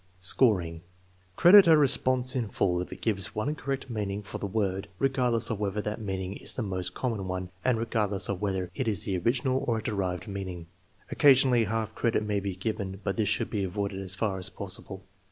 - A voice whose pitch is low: Yes, low, 105 Hz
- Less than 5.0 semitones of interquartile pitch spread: Yes, average, 3.7 semitones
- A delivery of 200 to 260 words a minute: Yes, fast, 205 wpm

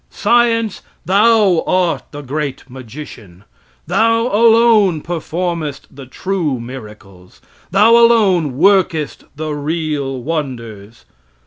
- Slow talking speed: Yes, slow, 95 wpm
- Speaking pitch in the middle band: Yes, medium, 155 Hz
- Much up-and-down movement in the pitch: Yes, wide, 7.1 semitones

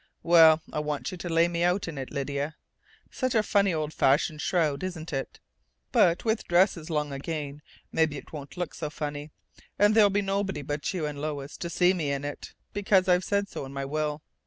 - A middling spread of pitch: Yes, average, 3.9 semitones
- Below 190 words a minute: No, fast, 205 wpm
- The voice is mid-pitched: Yes, medium, 160 Hz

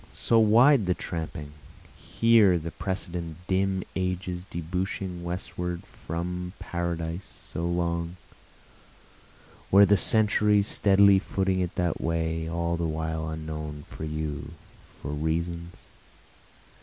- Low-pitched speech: Yes, very low, 85 Hz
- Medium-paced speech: No, slow, 110 wpm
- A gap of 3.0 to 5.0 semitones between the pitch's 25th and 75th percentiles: No, narrow, 2.5 semitones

